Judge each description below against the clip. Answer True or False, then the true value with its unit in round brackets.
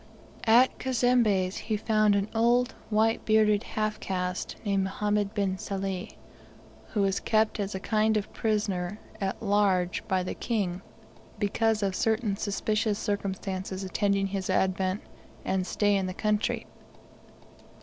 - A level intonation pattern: True (2.1 semitones)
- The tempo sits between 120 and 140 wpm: True (135 wpm)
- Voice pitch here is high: True (205 Hz)